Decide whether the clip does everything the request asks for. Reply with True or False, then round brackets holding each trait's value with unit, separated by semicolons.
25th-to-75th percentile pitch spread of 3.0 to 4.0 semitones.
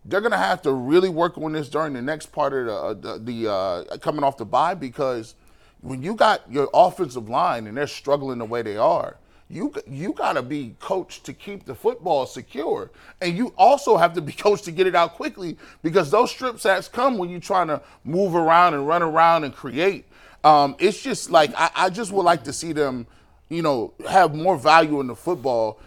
False (4.7 semitones)